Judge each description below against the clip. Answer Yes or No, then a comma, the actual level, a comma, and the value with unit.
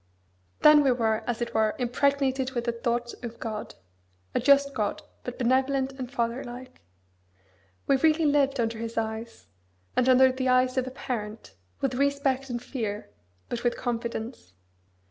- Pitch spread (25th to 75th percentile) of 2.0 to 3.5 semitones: Yes, narrow, 2.5 semitones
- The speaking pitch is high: Yes, very high, 250 Hz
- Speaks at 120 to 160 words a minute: Yes, average, 155 wpm